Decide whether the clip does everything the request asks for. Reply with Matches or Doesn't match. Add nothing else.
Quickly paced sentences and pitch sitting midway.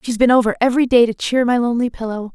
Doesn't match